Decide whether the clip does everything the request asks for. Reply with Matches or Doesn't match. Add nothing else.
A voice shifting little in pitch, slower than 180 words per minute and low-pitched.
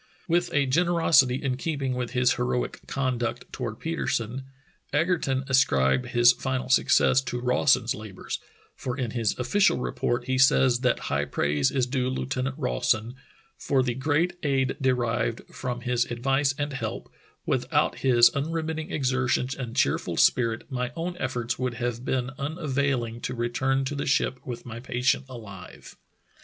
Matches